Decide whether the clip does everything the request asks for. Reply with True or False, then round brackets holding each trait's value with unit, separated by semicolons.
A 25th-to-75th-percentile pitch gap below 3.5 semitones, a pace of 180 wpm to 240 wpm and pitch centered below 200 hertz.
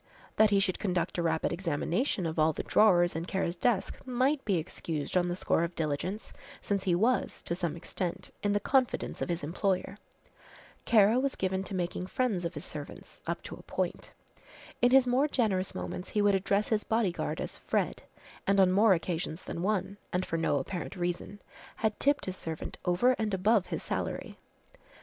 False (3.8 semitones; 190 wpm; 190 Hz)